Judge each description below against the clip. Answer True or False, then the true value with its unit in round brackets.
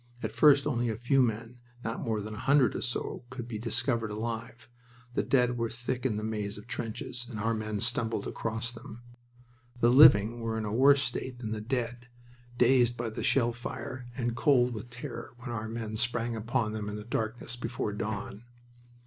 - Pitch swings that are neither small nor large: False (2.0 semitones)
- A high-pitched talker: False (115 Hz)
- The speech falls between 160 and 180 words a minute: False (195 wpm)